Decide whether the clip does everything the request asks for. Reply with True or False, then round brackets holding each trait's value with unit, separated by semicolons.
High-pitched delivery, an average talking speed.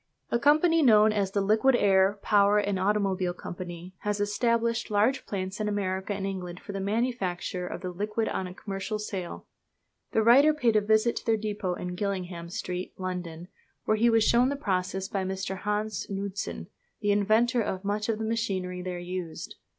True (205 Hz; 180 wpm)